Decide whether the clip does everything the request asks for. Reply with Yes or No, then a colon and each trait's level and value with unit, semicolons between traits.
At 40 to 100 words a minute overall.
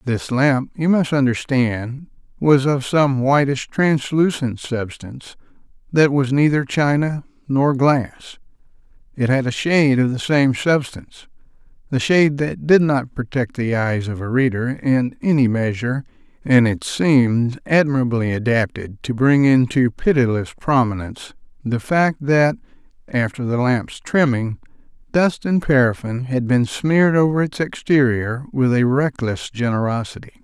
No: slow, 135 wpm